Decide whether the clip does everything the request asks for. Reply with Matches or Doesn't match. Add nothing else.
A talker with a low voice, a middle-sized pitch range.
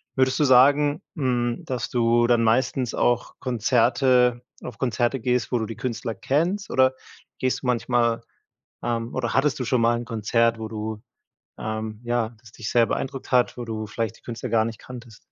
Doesn't match